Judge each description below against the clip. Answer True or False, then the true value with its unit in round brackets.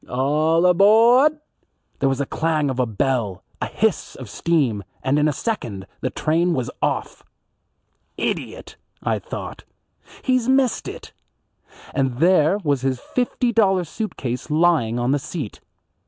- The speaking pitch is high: False (150 Hz)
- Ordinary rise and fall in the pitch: False (6.6 semitones)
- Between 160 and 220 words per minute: False (145 wpm)